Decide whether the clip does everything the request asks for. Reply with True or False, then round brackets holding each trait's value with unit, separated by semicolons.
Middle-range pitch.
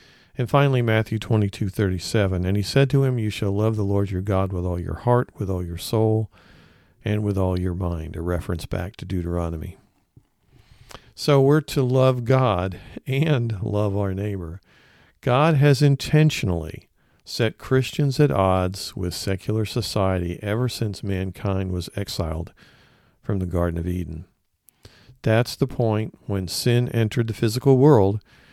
False (105 Hz)